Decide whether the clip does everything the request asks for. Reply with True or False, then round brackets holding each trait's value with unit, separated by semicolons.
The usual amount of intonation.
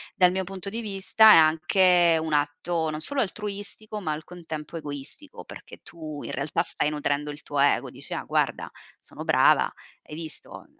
True (4.2 semitones)